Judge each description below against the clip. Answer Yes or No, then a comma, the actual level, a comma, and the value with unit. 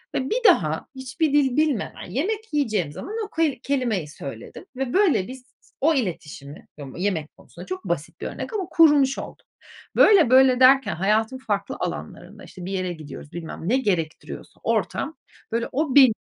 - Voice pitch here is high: Yes, high, 245 Hz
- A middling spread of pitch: No, wide, 7.9 semitones